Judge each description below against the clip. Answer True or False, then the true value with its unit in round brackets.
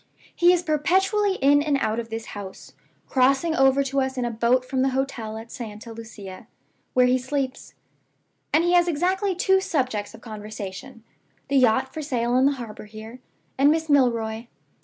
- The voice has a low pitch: False (260 Hz)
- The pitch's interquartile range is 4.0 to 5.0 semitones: True (4.4 semitones)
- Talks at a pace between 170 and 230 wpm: True (180 wpm)